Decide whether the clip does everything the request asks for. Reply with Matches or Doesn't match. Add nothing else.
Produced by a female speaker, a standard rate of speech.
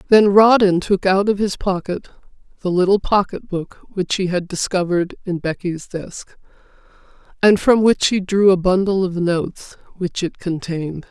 Matches